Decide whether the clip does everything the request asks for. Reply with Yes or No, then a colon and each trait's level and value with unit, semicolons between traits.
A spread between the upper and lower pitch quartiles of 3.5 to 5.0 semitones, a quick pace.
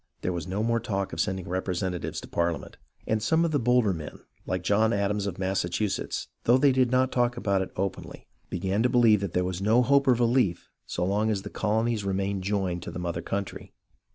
Yes: average, 4.1 semitones; fast, 210 wpm